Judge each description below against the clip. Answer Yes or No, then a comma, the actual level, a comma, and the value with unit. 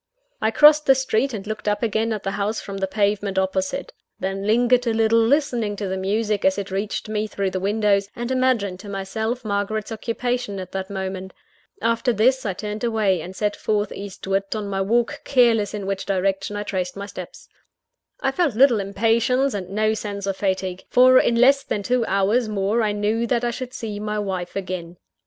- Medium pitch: No, high, 210 Hz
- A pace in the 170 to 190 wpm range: No, average, 200 wpm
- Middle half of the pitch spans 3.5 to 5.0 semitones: No, average, 2.9 semitones